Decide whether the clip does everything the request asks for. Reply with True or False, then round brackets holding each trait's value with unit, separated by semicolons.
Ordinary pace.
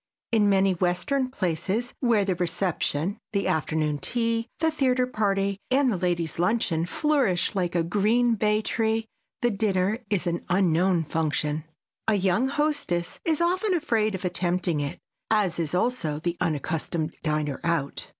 True (150 wpm)